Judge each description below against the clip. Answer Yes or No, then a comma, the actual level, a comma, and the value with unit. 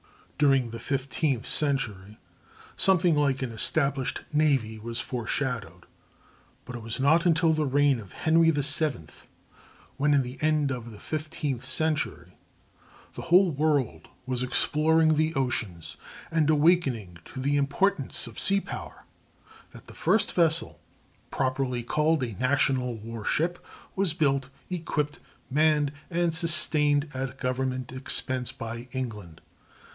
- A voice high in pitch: No, medium, 140 Hz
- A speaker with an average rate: No, slow, 130 wpm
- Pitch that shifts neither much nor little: Yes, average, 4.0 semitones